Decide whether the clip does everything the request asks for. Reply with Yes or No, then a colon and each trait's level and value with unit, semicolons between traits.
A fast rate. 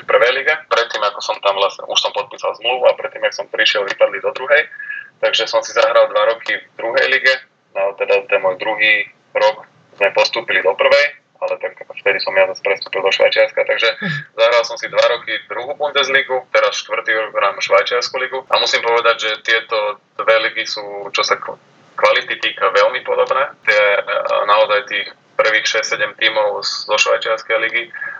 Yes: fast, 185 wpm